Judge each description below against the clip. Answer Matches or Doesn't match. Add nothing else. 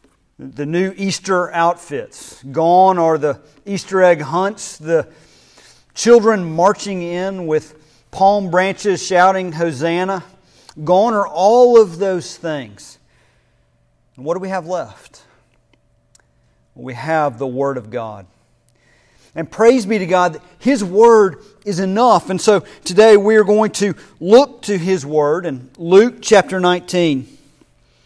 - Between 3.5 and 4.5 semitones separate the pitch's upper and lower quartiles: Doesn't match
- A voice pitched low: Doesn't match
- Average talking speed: Doesn't match